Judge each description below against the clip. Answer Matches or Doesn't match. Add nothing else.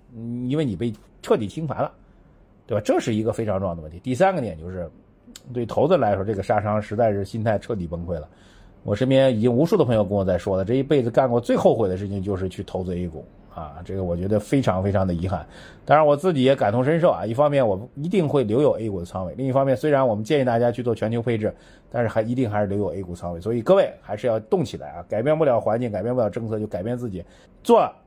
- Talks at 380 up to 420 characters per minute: Matches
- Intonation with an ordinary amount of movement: Matches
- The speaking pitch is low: Matches